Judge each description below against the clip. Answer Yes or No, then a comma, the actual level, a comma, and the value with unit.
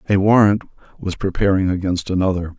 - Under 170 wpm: Yes, average, 140 wpm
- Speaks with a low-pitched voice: Yes, very low, 95 Hz